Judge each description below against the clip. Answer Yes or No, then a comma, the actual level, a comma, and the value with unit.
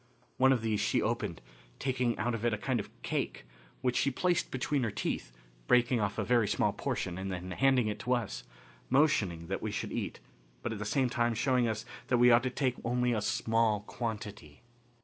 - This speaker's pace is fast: Yes, fast, 210 wpm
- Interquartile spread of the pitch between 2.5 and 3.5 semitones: Yes, average, 3.0 semitones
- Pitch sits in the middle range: No, low, 120 Hz